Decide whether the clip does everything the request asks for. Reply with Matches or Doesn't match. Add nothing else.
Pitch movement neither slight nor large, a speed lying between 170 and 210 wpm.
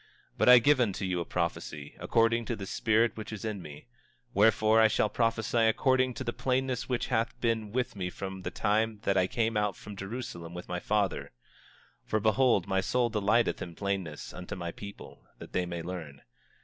Matches